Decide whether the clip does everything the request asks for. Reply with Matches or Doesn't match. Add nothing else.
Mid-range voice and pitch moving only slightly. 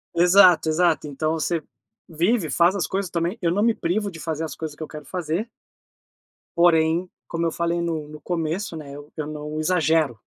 Matches